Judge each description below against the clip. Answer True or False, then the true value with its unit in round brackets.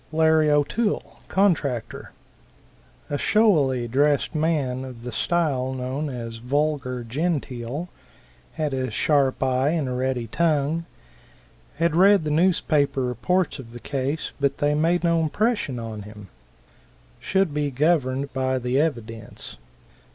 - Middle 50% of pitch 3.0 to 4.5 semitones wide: True (4.0 semitones)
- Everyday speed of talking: False (130 wpm)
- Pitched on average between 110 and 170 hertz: True (140 Hz)